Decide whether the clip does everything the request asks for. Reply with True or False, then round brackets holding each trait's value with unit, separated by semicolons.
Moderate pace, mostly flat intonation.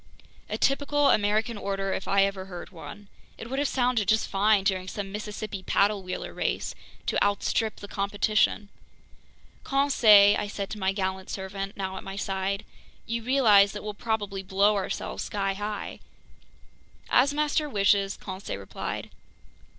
True (150 wpm; 1.9 semitones)